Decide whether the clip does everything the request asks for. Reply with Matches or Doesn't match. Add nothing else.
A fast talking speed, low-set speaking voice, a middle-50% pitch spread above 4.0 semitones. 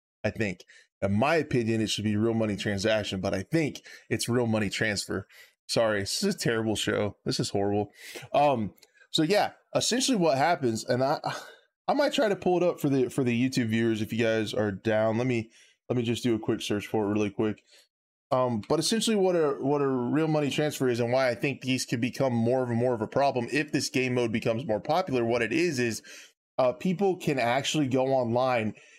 Matches